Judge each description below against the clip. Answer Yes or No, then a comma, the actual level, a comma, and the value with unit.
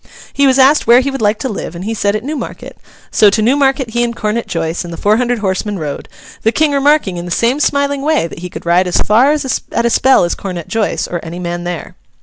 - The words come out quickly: Yes, fast, 250 wpm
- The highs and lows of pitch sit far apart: Yes, wide, 6.9 semitones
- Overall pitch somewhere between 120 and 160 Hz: No, high, 225 Hz